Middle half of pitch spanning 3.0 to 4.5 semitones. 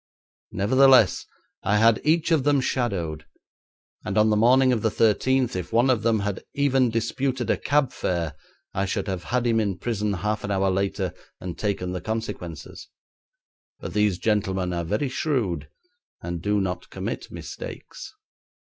No: average, 5.0 semitones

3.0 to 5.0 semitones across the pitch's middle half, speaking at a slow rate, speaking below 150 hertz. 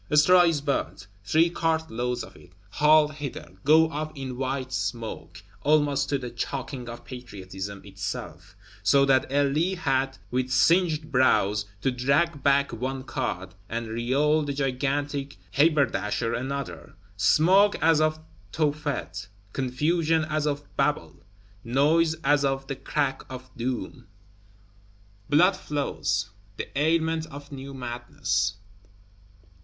Yes: average, 3.7 semitones; slow, 125 wpm; medium, 140 Hz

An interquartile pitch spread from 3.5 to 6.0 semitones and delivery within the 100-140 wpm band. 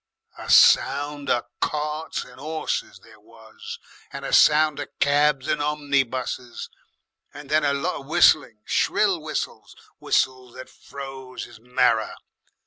No: narrow, 2.5 semitones; slow, 135 wpm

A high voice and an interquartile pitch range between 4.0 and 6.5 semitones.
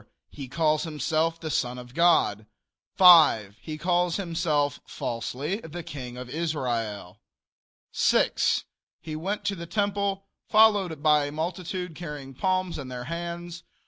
No: medium, 160 Hz; average, 4.6 semitones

